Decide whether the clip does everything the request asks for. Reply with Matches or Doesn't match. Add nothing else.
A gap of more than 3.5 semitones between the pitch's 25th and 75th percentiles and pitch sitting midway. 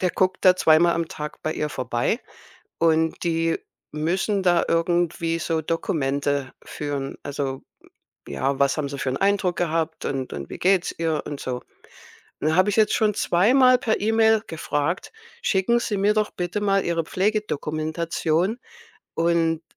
Matches